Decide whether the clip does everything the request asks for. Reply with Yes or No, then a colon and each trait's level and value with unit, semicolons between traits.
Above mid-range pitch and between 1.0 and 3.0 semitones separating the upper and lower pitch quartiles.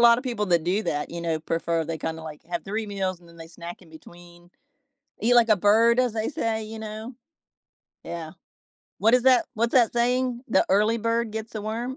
No: high, 215 Hz; average, 5.3 semitones